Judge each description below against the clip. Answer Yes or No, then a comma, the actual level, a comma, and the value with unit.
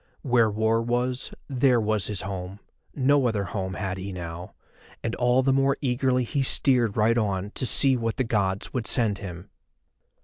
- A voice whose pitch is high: No, low, 115 Hz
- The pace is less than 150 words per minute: No, average, 175 wpm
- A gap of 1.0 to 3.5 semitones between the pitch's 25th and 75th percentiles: No, average, 4.3 semitones